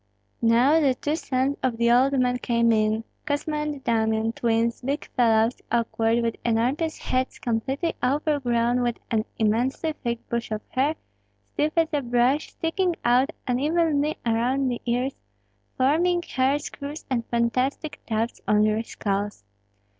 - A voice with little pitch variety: No, average, 3.7 semitones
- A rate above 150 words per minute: No, average, 145 wpm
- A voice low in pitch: No, very high, 250 Hz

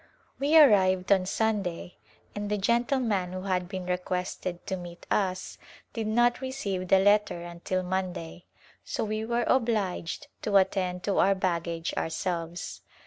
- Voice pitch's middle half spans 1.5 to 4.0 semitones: Yes, average, 3.1 semitones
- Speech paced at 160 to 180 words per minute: No, average, 140 wpm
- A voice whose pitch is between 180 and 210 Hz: Yes, high, 190 Hz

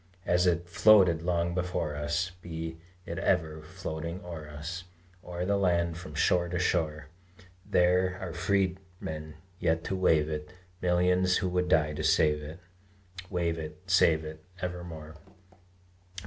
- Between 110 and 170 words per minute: Yes, average, 140 wpm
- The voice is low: Yes, very low, 85 Hz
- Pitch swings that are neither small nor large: No, narrow, 2.3 semitones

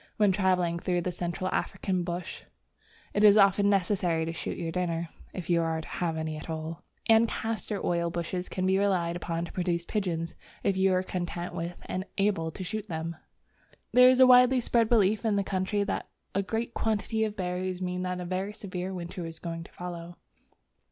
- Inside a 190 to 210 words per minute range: Yes, average, 200 wpm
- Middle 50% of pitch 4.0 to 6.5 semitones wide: No, average, 2.9 semitones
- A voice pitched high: No, medium, 180 Hz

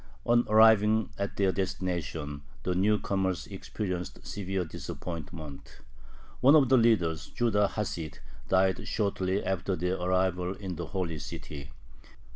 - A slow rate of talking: Yes, slow, 125 wpm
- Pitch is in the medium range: No, very low, 95 Hz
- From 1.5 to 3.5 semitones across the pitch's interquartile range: Yes, average, 3.0 semitones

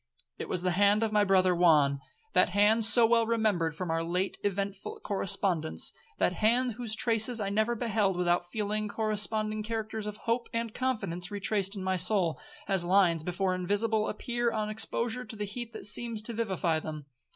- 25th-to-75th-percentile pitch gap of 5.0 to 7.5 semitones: No, average, 3.4 semitones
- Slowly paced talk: No, average, 175 wpm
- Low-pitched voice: No, high, 205 Hz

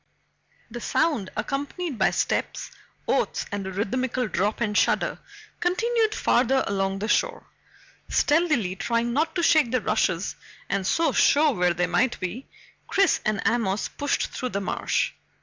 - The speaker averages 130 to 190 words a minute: Yes, average, 150 wpm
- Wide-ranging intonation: Yes, wide, 7.2 semitones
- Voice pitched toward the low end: No, high, 235 Hz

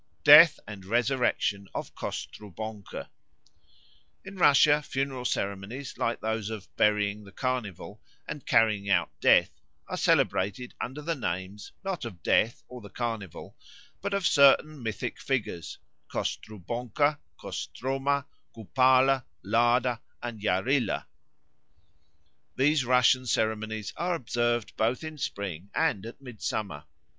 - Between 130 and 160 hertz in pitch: No, low, 120 Hz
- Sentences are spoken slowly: Yes, slow, 115 wpm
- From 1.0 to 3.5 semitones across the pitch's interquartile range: No, average, 4.5 semitones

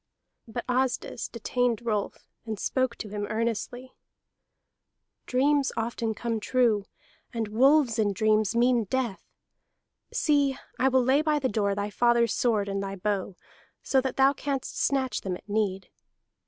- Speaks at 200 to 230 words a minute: No, average, 145 wpm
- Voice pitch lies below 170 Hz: No, high, 235 Hz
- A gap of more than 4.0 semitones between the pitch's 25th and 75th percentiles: No, average, 3.7 semitones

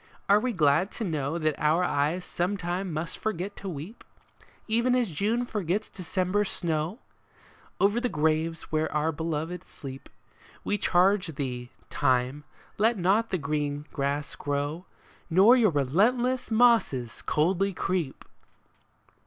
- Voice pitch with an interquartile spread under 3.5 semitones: No, wide, 5.4 semitones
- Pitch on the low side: No, medium, 175 Hz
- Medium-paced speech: No, slow, 130 wpm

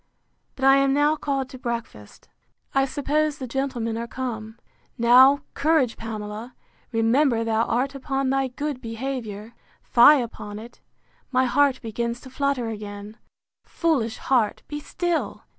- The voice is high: Yes, very high, 255 Hz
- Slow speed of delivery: Yes, slow, 125 wpm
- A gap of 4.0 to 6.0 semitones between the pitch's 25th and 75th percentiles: No, average, 3.3 semitones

